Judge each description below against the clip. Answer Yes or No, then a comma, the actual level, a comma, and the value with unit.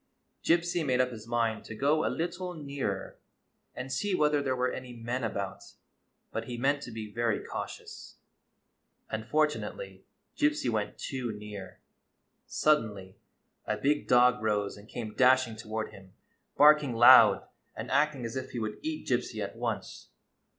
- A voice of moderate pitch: No, low, 125 Hz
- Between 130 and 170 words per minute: Yes, average, 155 wpm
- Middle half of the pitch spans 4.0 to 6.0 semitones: Yes, average, 4.9 semitones